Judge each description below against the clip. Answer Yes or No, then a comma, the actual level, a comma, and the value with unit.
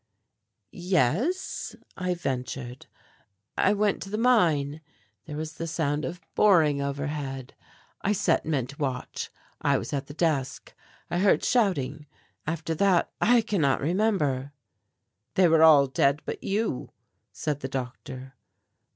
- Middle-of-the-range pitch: Yes, medium, 155 Hz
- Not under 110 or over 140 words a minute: Yes, slow, 135 wpm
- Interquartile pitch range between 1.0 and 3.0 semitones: No, average, 5.2 semitones